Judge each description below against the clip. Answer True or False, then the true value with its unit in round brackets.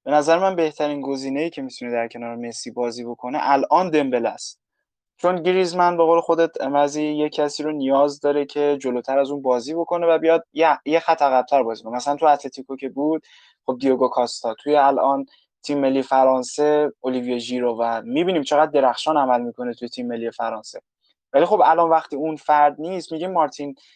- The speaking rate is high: True (185 wpm)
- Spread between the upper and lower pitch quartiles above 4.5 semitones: False (3.8 semitones)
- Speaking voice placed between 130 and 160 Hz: True (140 Hz)